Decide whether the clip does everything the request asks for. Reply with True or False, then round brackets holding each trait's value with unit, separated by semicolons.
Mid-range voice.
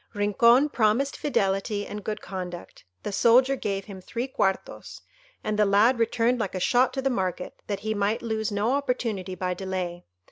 False (210 Hz)